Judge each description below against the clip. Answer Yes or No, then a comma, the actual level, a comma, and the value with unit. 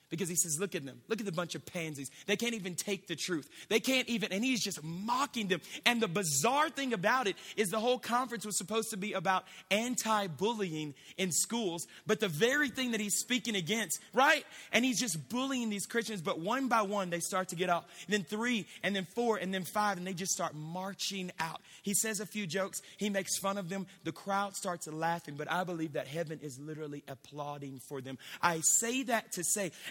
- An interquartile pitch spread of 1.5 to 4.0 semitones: No, average, 4.5 semitones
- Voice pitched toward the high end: Yes, high, 195 Hz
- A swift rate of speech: Yes, fast, 225 wpm